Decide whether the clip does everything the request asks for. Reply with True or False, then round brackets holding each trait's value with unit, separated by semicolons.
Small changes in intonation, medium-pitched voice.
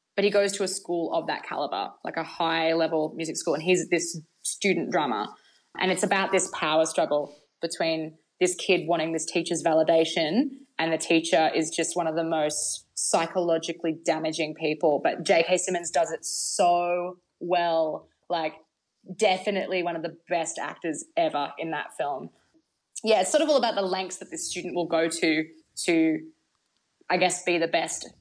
True (2.3 semitones; 170 Hz)